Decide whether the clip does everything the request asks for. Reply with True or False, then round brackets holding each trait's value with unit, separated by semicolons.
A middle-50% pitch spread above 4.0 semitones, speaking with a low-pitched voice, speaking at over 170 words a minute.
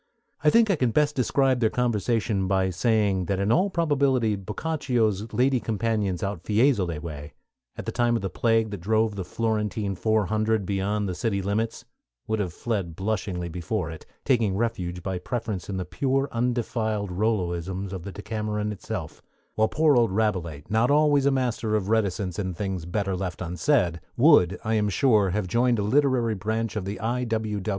False (3.7 semitones; 105 Hz; 180 wpm)